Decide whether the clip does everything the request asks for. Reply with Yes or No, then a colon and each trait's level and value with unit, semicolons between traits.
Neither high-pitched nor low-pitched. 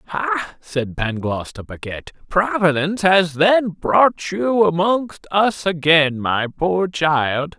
Yes: medium, 165 Hz